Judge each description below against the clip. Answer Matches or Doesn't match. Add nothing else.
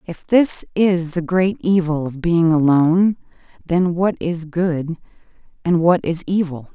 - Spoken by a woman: Matches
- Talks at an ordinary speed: Matches